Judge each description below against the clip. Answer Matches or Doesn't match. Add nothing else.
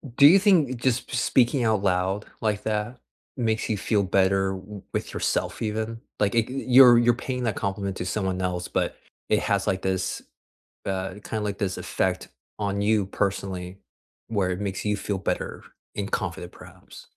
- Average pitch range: Matches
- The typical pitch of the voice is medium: Doesn't match